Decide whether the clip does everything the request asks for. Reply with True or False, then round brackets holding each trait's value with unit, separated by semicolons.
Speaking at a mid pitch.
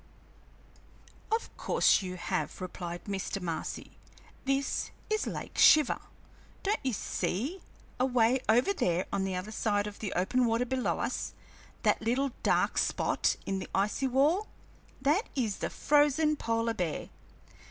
False (230 Hz)